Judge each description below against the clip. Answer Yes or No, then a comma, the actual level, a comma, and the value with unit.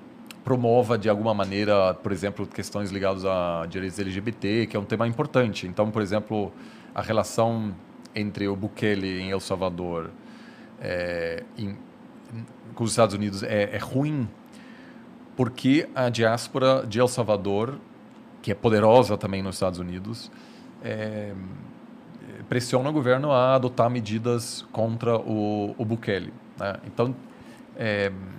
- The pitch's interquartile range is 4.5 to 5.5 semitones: No, average, 3.4 semitones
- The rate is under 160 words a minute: Yes, average, 135 wpm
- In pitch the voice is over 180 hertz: No, low, 110 Hz